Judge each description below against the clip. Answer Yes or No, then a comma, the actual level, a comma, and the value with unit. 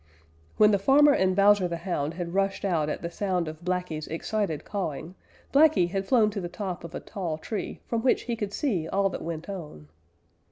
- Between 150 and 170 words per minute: No, fast, 205 wpm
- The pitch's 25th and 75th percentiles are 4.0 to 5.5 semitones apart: No, average, 3.6 semitones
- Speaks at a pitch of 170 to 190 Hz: Yes, medium, 185 Hz